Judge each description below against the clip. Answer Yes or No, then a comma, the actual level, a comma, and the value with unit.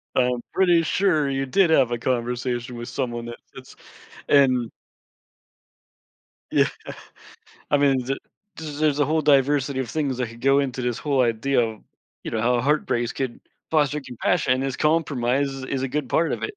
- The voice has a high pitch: No, low, 135 Hz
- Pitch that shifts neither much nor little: Yes, average, 3.0 semitones